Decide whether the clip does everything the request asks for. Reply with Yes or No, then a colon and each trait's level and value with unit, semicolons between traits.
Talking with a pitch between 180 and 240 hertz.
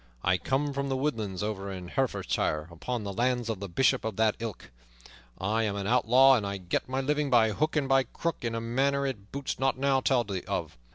No: low, 120 Hz